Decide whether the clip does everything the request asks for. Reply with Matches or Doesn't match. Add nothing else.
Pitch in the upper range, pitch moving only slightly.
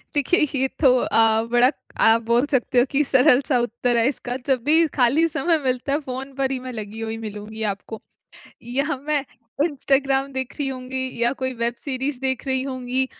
Matches